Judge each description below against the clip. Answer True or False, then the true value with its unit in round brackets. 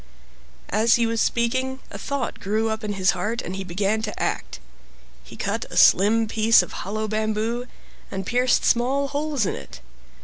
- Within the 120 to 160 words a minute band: False (175 wpm)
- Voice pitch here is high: True (220 Hz)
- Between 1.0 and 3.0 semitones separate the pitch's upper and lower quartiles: True (2.7 semitones)